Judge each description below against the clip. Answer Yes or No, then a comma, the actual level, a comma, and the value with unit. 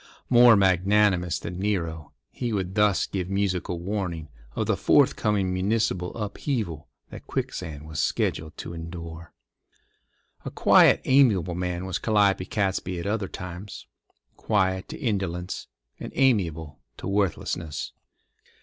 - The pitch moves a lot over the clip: No, average, 3.4 semitones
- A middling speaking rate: No, slow, 120 wpm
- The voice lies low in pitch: Yes, very low, 95 Hz